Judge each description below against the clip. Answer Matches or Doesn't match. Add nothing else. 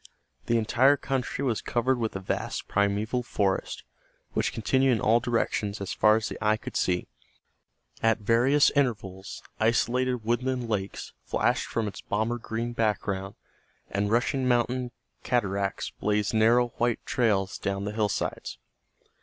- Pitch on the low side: Matches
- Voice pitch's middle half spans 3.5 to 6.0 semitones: Doesn't match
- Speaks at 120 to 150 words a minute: Matches